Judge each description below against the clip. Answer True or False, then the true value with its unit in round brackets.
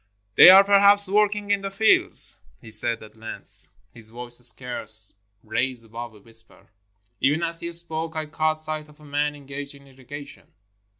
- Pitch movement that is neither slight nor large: False (6.1 semitones)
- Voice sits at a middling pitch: True (145 Hz)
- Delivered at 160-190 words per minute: True (170 wpm)